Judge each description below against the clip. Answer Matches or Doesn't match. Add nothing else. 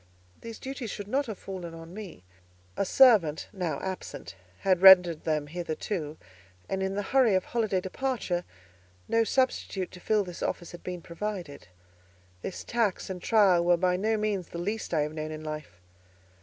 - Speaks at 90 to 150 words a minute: Doesn't match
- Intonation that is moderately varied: Matches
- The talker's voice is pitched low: Doesn't match